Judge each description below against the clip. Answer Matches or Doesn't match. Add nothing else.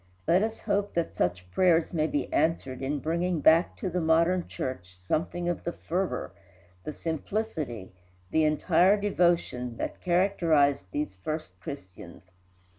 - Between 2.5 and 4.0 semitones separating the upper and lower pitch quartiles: Doesn't match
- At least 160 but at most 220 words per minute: Doesn't match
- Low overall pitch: Doesn't match